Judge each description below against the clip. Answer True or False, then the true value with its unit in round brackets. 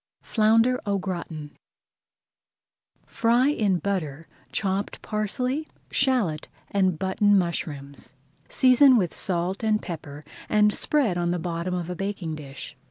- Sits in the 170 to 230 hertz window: True (190 Hz)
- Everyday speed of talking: False (120 wpm)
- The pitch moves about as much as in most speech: True (4.4 semitones)